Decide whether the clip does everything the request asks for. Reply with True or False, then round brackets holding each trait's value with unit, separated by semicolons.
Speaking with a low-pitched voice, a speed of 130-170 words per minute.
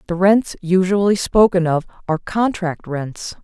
False (185 Hz; 140 wpm)